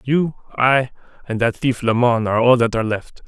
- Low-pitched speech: Yes, low, 120 Hz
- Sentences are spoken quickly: Yes, fast, 220 wpm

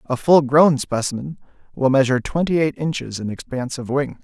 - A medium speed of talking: Yes, average, 185 wpm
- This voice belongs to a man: Yes, male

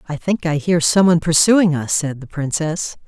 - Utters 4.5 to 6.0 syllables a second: Yes, 5.0 syllables/s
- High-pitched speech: No, medium, 165 Hz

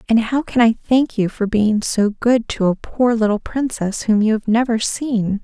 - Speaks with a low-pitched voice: No, high, 225 Hz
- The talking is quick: Yes, fast, 220 wpm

